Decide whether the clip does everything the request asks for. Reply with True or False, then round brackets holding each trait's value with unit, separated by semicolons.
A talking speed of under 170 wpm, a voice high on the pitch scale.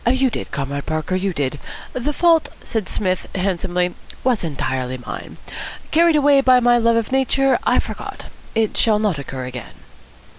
True (160 wpm; 210 Hz)